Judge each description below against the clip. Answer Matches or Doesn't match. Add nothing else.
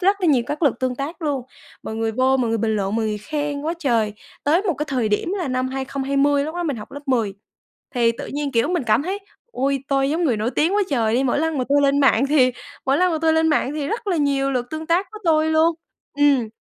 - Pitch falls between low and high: Doesn't match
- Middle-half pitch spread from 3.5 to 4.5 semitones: Matches